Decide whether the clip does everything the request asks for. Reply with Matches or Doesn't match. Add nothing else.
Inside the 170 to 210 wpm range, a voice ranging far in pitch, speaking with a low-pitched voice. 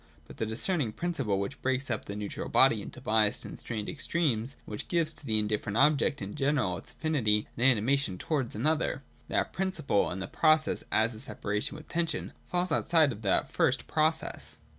Matches